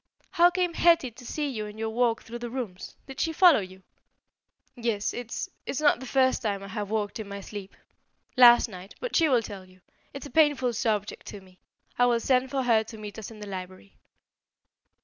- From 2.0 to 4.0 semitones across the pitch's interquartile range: No, average, 4.4 semitones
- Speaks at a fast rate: Yes, fast, 210 wpm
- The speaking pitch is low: No, high, 230 Hz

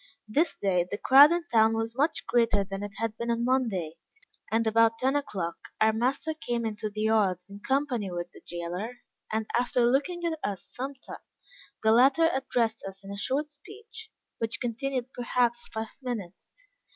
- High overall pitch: Yes, high, 230 Hz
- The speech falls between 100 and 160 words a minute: No, average, 175 wpm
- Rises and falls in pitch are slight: No, average, 4.2 semitones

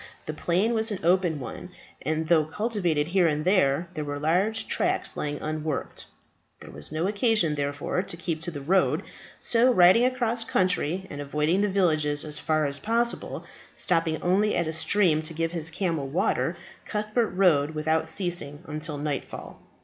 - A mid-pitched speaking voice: Yes, medium, 165 Hz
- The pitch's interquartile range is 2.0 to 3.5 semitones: No, average, 4.1 semitones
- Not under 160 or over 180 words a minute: Yes, average, 170 wpm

